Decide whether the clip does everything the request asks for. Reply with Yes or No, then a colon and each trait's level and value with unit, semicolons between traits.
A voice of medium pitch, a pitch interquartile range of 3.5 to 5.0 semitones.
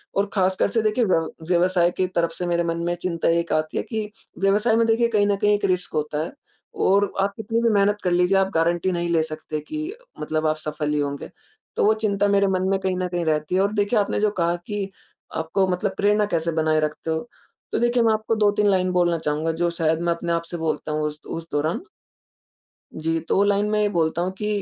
Yes: medium, 180 Hz; average, 3.9 semitones